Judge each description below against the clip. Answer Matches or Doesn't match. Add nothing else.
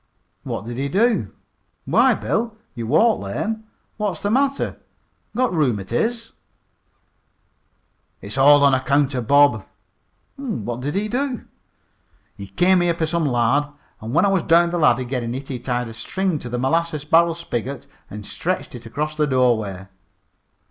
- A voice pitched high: Doesn't match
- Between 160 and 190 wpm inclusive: Doesn't match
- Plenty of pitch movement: Matches